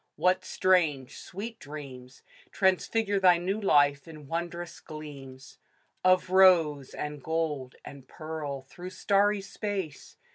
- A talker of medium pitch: Yes, medium, 165 Hz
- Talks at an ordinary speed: No, slow, 115 wpm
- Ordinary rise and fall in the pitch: Yes, average, 4.6 semitones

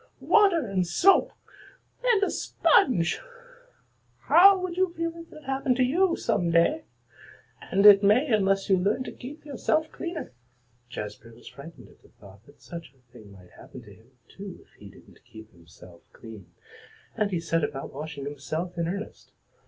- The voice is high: Yes, high, 195 Hz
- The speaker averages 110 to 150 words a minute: No, average, 170 wpm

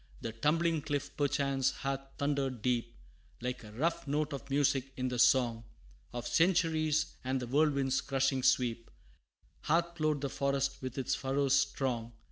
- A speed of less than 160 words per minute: Yes, average, 150 wpm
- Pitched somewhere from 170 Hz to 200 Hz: No, low, 135 Hz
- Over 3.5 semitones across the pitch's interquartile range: No, narrow, 2.5 semitones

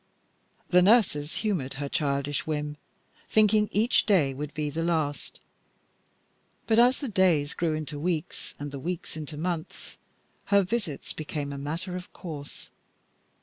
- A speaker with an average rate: Yes, average, 145 wpm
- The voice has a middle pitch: Yes, medium, 160 Hz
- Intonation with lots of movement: No, average, 4.3 semitones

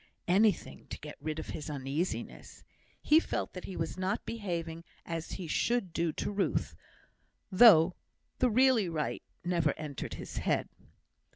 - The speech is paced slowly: No, average, 150 wpm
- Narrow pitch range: No, average, 4.5 semitones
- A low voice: No, medium, 175 Hz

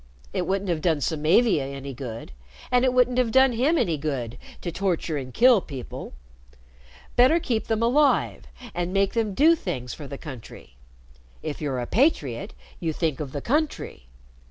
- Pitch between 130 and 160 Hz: No, medium, 175 Hz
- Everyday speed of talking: Yes, average, 170 wpm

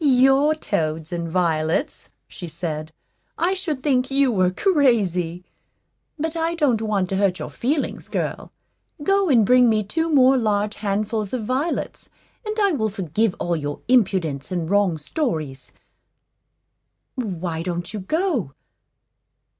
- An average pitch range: No, wide, 7.7 semitones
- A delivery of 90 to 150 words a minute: Yes, average, 140 wpm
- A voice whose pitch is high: Yes, high, 215 Hz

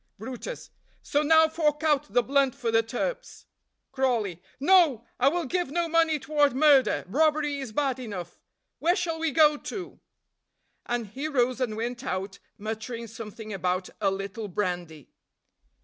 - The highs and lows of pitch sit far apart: Yes, wide, 5.8 semitones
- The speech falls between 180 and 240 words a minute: No, average, 150 wpm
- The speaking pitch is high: Yes, very high, 260 Hz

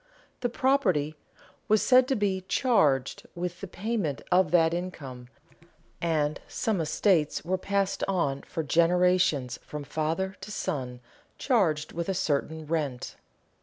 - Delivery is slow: Yes, slow, 130 wpm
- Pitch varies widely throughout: No, average, 4.5 semitones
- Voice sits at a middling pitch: Yes, medium, 175 Hz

